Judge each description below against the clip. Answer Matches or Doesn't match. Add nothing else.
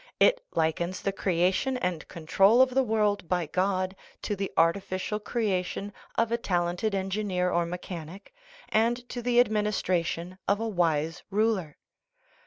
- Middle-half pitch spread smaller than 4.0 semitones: Matches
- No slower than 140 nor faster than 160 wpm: Matches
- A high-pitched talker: Matches